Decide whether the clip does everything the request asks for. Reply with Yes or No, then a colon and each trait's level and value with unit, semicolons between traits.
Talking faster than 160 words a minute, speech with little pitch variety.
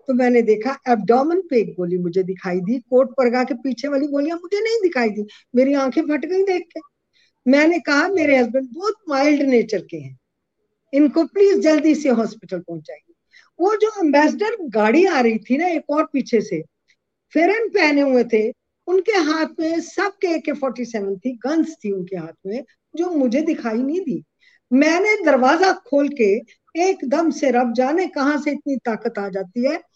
No: average, 180 wpm; wide, 5.6 semitones